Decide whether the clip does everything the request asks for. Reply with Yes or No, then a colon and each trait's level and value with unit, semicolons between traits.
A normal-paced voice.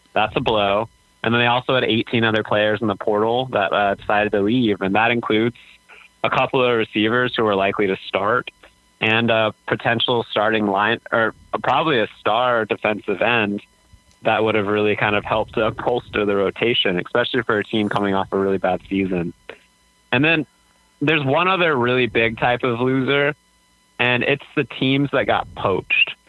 Yes: average, 185 wpm